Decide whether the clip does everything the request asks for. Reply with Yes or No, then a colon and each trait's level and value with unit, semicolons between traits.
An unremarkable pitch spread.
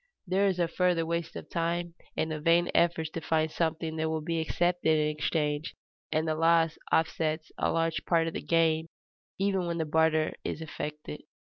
No: narrow, 1.2 semitones